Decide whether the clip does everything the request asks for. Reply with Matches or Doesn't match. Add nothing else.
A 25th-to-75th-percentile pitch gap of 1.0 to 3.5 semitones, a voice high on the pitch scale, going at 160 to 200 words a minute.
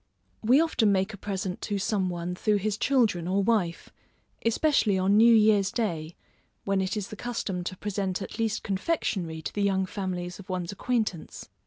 Matches